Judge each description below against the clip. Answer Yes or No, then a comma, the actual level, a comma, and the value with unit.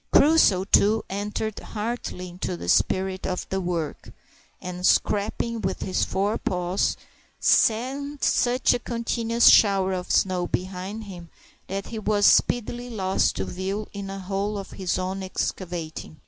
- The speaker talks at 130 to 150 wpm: Yes, average, 140 wpm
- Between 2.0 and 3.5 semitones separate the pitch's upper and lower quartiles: Yes, average, 3.1 semitones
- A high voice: Yes, high, 195 Hz